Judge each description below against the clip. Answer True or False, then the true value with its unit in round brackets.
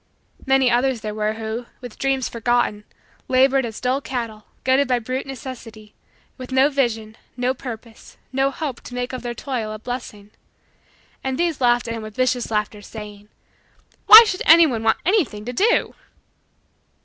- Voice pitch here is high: True (245 Hz)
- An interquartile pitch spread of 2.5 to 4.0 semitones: True (3.3 semitones)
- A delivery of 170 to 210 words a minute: False (160 wpm)